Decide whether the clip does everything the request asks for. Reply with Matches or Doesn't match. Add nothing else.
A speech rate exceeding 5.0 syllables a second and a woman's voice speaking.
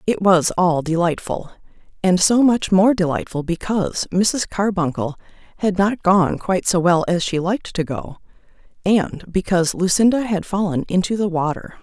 Doesn't match